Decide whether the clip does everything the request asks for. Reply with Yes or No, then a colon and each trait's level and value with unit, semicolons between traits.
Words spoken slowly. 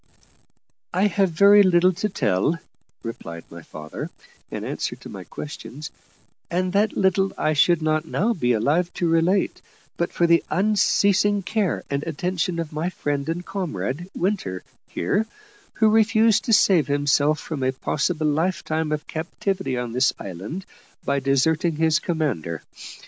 No: average, 150 wpm